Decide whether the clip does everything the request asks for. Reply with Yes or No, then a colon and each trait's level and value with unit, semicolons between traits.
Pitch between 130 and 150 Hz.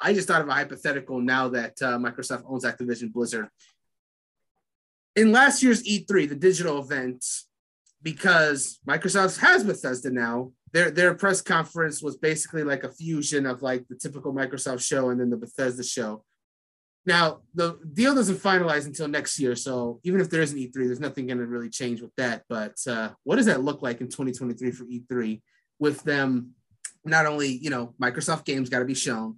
Yes: low, 135 Hz